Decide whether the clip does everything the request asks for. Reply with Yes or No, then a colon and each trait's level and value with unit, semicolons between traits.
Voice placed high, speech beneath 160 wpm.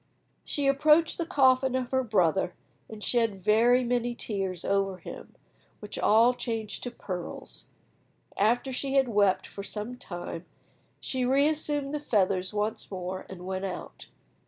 Yes: high, 225 Hz; average, 145 wpm